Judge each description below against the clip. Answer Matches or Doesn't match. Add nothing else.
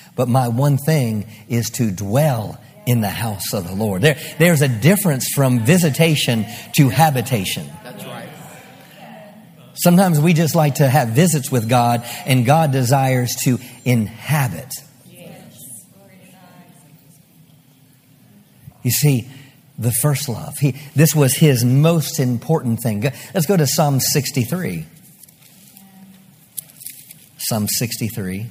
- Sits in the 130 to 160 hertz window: Matches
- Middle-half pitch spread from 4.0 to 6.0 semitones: Matches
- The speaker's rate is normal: Doesn't match